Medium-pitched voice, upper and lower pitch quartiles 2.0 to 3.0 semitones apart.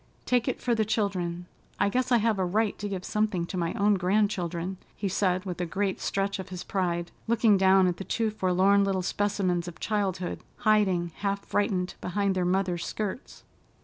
No: high, 195 Hz; narrow, 2.4 semitones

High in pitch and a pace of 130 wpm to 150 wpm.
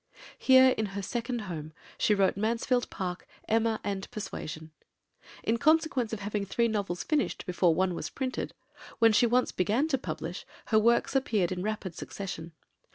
No: high, 215 Hz; average, 160 wpm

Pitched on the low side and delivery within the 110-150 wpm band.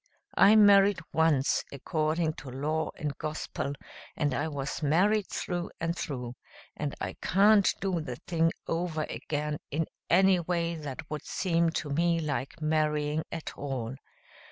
No: medium, 155 Hz; average, 145 wpm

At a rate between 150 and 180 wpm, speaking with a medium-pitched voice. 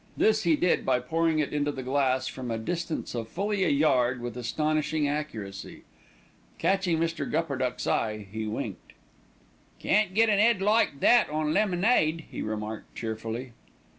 Yes: average, 160 wpm; medium, 150 Hz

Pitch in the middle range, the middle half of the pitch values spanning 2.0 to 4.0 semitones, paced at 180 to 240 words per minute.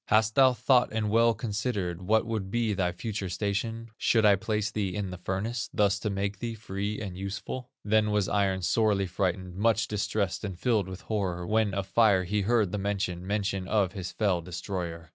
No: low, 100 Hz; narrow, 2.6 semitones; average, 195 wpm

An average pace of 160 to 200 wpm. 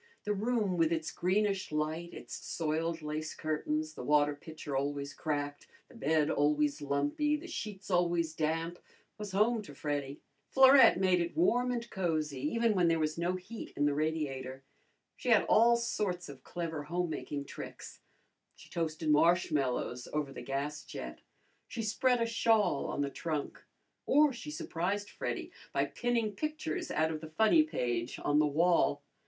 Yes: average, 165 wpm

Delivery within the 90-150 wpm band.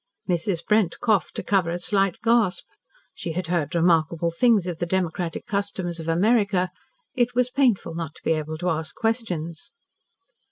No: average, 165 wpm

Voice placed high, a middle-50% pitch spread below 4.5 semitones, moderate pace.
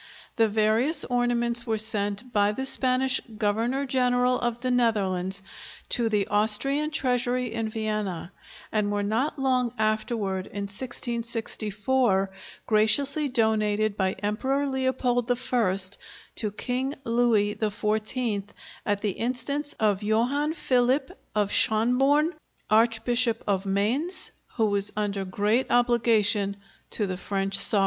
No: high, 225 Hz; average, 3.4 semitones; slow, 120 wpm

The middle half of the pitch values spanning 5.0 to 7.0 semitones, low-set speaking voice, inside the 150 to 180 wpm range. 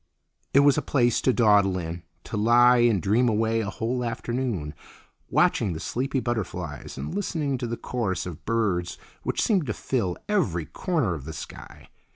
Yes: wide, 5.5 semitones; low, 115 Hz; average, 175 wpm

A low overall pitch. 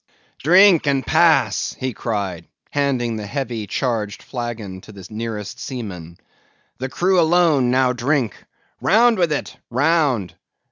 Yes: low, 125 Hz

